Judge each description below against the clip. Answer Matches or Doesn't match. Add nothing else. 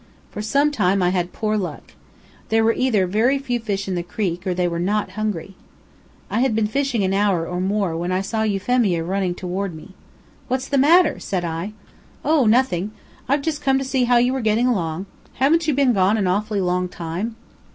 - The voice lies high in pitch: Matches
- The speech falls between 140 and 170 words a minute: Doesn't match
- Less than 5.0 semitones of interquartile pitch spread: Doesn't match